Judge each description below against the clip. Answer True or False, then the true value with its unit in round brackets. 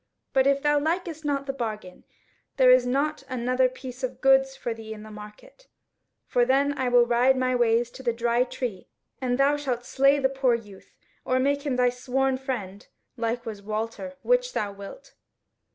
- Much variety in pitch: False (2.7 semitones)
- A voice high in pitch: True (255 Hz)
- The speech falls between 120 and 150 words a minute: False (195 wpm)